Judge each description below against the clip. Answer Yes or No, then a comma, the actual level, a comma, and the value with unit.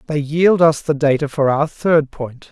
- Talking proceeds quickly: Yes, fast, 215 wpm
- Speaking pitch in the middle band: Yes, medium, 150 Hz